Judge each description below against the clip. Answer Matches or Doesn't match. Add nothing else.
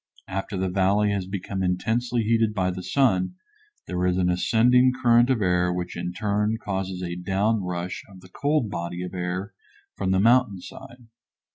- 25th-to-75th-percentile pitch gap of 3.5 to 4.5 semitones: Matches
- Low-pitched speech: Matches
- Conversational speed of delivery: Matches